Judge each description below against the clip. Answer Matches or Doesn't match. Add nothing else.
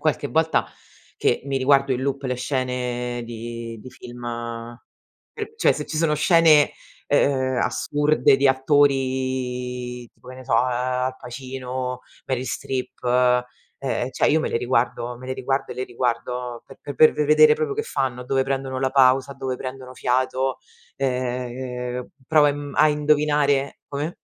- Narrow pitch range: Matches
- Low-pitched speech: Matches